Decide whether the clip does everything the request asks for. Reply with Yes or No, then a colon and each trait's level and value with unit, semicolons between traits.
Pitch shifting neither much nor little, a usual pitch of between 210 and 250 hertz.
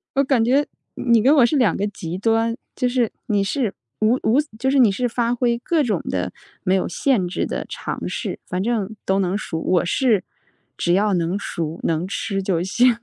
Yes: average, 4.8 semitones; high, 215 Hz